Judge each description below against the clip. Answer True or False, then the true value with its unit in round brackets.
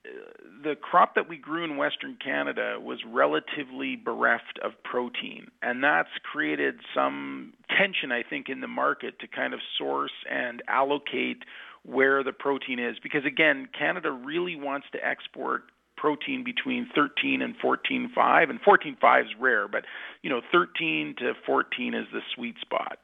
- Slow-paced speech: False (155 wpm)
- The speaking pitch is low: False (155 Hz)